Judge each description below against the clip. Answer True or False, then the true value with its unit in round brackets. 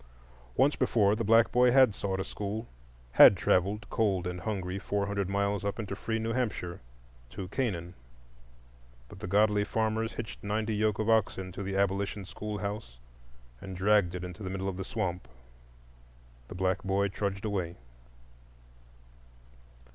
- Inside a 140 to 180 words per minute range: True (155 wpm)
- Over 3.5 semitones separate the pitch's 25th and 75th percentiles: False (2.4 semitones)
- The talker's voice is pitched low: True (100 Hz)